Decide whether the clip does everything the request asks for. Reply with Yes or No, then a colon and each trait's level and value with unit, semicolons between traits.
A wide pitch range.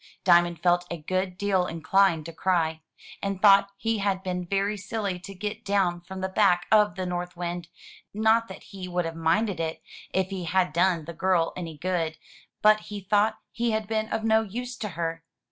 No: average, 3.0 semitones